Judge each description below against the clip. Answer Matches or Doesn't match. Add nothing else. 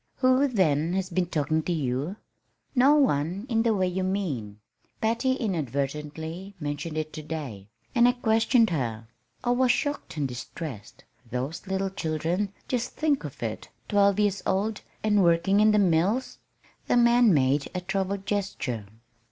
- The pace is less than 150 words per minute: Doesn't match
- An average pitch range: Doesn't match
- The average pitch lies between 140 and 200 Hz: Matches